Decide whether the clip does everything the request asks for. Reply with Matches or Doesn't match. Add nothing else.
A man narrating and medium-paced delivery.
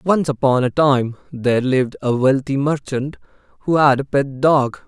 Matches